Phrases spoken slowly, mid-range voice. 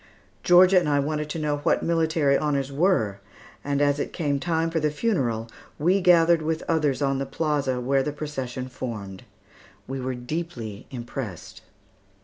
No: average, 160 wpm; medium, 145 Hz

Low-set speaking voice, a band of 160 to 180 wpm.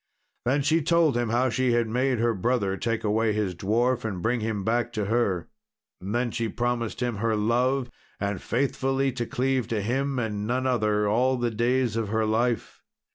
No: low, 120 Hz; average, 190 wpm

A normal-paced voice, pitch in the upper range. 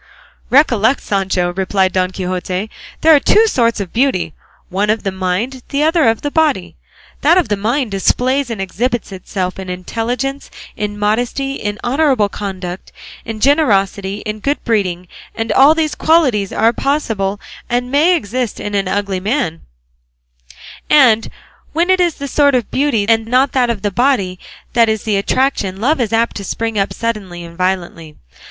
Yes: average, 170 wpm; high, 225 Hz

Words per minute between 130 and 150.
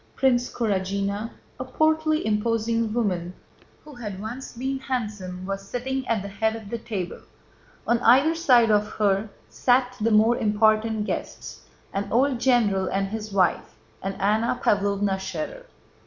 Yes: average, 140 wpm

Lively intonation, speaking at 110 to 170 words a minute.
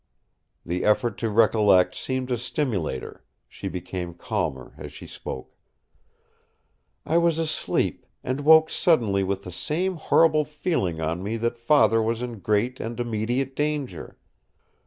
Yes: wide, 7.1 semitones; average, 140 wpm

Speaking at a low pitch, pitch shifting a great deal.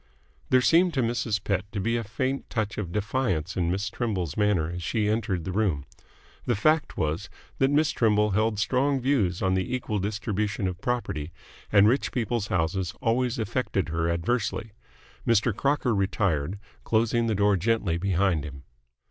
No: low, 105 Hz; average, 4.2 semitones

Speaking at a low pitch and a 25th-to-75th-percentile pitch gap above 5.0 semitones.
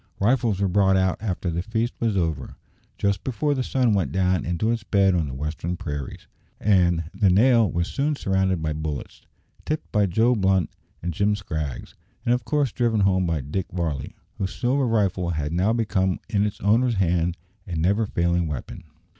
No: very low, 95 Hz; average, 4.5 semitones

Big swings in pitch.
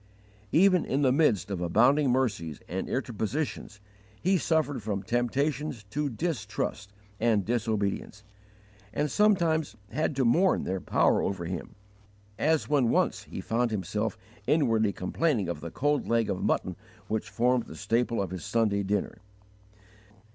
Yes: wide, 6.2 semitones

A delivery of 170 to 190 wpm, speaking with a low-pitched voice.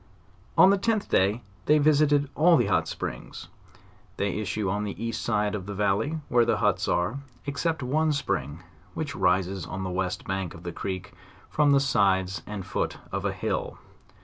Yes: average, 175 wpm; low, 105 Hz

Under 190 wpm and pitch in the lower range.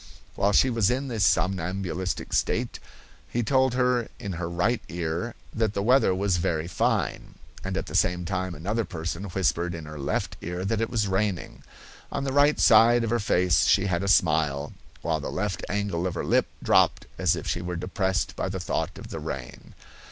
No: average, 195 wpm; very low, 95 Hz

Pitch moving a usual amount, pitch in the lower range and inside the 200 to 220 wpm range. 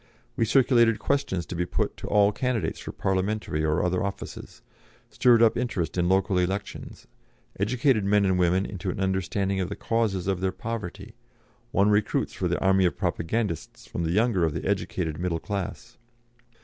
No: average, 3.4 semitones; very low, 95 Hz; average, 175 wpm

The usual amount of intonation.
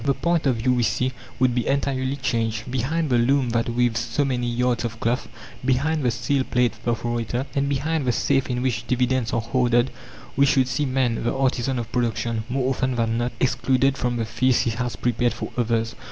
No: narrow, 2.0 semitones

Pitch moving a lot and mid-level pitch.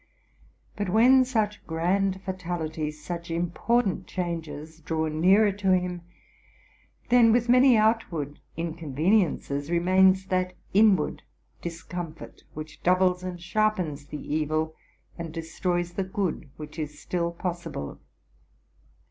No: average, 3.3 semitones; medium, 175 Hz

